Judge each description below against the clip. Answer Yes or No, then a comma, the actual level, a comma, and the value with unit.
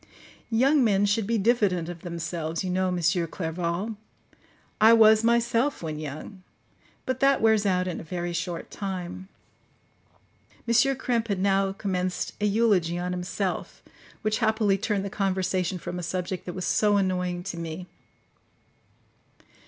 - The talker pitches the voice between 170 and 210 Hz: Yes, high, 190 Hz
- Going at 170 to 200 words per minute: No, average, 145 wpm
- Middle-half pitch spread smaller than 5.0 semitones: Yes, average, 3.5 semitones